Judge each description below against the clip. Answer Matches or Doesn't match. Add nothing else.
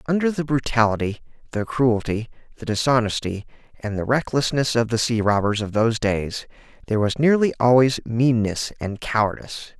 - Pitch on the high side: Doesn't match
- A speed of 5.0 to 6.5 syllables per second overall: Matches